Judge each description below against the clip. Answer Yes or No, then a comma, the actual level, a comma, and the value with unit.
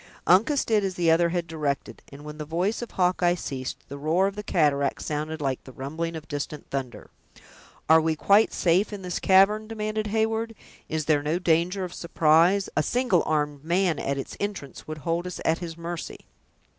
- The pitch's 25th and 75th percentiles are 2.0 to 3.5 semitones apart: No, average, 4.2 semitones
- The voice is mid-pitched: Yes, medium, 170 Hz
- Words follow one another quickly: No, average, 195 wpm